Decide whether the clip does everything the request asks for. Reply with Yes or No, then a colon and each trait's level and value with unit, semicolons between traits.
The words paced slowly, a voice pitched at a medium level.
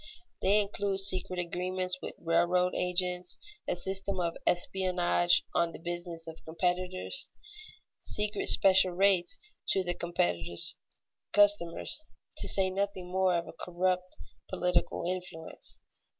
Yes: slow, 115 wpm; medium, 180 Hz